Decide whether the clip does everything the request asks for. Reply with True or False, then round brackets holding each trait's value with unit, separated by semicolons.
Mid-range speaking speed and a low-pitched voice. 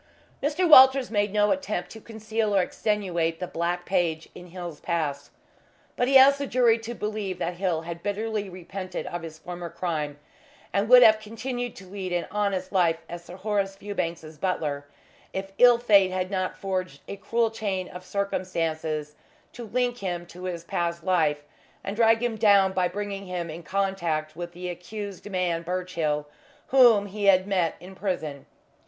False (170 wpm; 185 Hz)